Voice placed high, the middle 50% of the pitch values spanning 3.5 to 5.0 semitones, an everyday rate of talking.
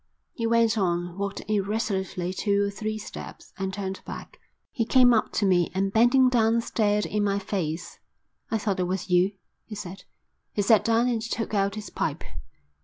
No: high, 205 Hz; average, 2.8 semitones; average, 180 wpm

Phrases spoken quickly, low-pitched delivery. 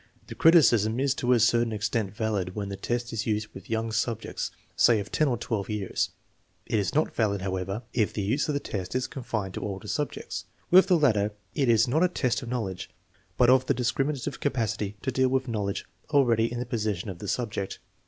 Yes: fast, 210 wpm; low, 115 Hz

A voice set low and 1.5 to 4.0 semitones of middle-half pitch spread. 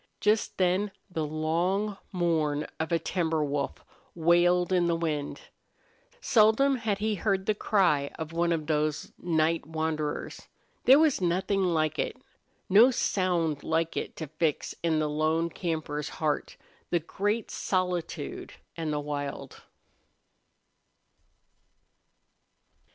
No: medium, 165 Hz; average, 3.4 semitones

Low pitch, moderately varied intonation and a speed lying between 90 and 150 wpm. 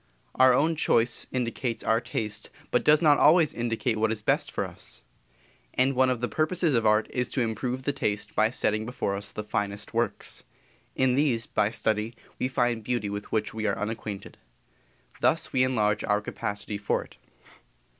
No: low, 115 Hz; average, 3.3 semitones; average, 180 wpm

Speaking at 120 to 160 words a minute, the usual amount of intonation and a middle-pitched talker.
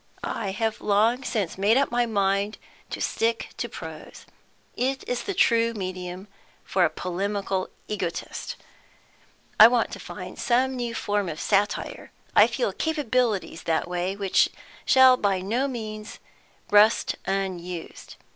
No: slow, 135 wpm; average, 3.7 semitones; high, 210 Hz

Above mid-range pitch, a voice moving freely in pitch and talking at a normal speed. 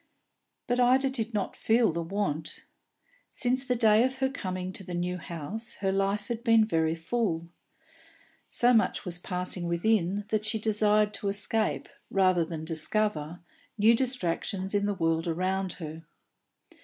No: high, 200 Hz; average, 4.4 semitones; average, 155 wpm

